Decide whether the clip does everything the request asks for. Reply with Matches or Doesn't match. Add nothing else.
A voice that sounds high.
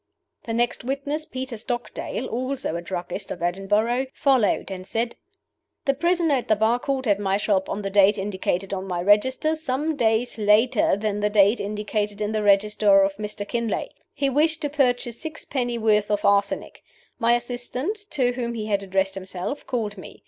Matches